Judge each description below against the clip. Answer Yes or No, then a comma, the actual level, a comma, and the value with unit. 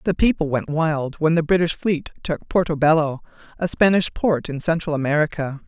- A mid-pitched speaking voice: Yes, medium, 160 Hz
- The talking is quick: No, average, 180 wpm